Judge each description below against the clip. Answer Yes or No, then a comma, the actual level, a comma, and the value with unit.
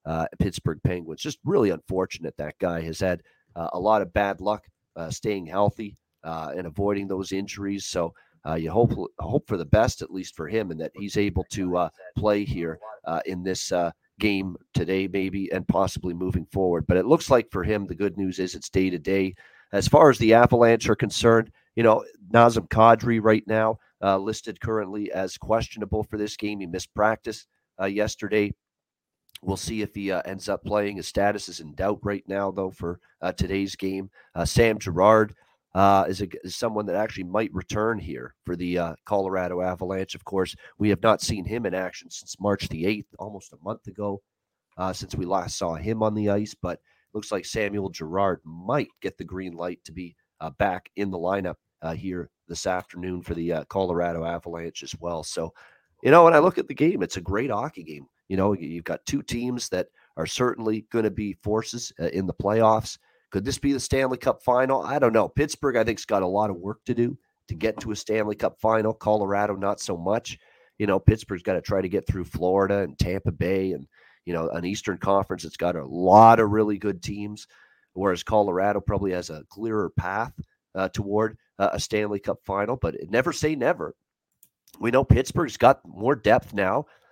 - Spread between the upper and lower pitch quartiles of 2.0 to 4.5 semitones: Yes, average, 2.9 semitones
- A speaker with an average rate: No, fast, 210 wpm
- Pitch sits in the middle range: No, low, 100 Hz